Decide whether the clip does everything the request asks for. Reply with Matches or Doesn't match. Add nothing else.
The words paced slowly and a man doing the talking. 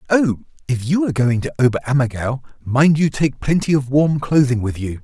Doesn't match